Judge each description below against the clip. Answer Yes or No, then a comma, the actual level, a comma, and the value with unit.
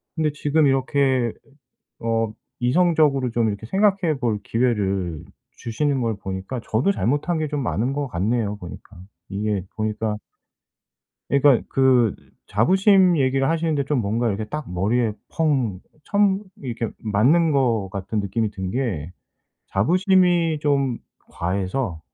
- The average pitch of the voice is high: No, low, 125 Hz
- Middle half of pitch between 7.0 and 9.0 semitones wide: No, wide, 6.0 semitones